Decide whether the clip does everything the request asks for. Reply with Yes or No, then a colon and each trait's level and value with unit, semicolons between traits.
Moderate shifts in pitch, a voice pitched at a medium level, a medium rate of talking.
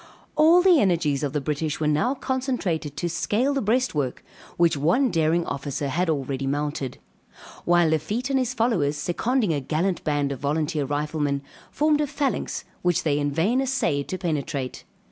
No: wide, 8.7 semitones; medium, 160 Hz; average, 165 wpm